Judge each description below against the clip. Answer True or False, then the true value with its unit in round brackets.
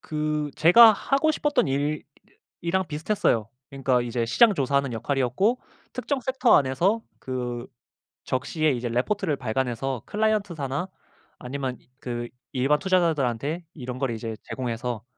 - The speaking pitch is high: False (140 Hz)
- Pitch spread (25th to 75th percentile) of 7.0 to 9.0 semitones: False (6.2 semitones)